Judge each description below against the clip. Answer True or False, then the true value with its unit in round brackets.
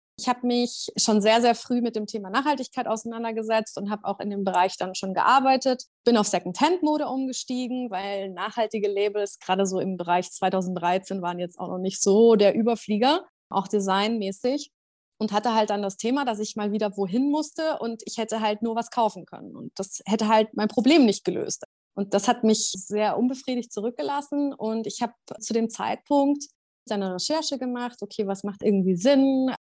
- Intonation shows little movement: False (3.9 semitones)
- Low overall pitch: False (220 Hz)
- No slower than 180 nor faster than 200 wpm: True (185 wpm)